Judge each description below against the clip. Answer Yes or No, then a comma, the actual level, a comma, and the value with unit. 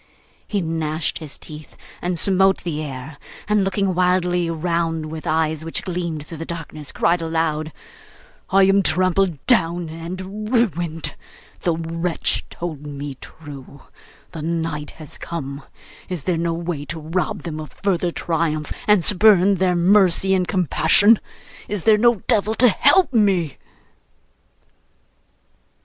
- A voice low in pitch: No, medium, 170 Hz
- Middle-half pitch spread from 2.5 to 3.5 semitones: Yes, average, 3.2 semitones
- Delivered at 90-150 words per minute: Yes, slow, 135 wpm